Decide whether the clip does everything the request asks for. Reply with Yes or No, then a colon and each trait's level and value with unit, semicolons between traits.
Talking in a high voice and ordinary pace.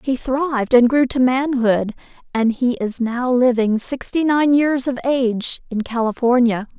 Yes: very high, 250 Hz; average, 160 wpm